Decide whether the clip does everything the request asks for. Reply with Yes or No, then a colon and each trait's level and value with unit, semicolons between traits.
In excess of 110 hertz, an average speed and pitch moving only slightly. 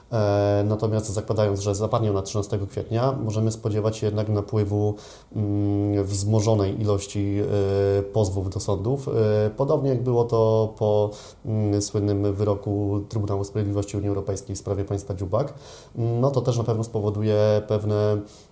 No: low, 105 Hz; average, 125 wpm; narrow, 1.4 semitones